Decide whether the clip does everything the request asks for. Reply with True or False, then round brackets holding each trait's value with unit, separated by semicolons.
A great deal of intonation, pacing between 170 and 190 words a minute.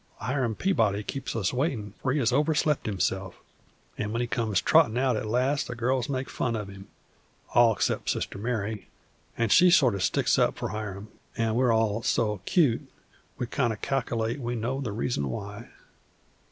False (3.5 semitones; 180 wpm)